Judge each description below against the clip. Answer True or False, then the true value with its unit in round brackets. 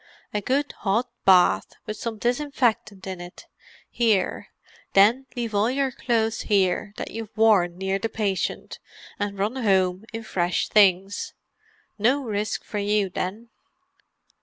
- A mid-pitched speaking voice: False (210 Hz)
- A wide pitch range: False (3.1 semitones)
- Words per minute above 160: False (135 wpm)